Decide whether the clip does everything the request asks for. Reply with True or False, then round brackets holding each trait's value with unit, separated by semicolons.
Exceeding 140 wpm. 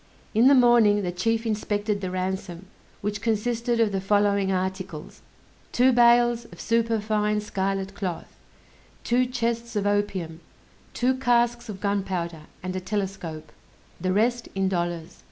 False (135 wpm)